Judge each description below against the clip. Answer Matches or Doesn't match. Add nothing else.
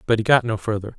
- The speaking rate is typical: Doesn't match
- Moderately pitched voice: Doesn't match